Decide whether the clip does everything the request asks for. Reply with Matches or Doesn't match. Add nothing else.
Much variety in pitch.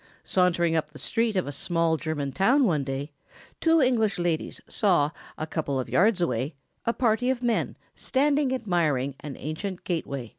Matches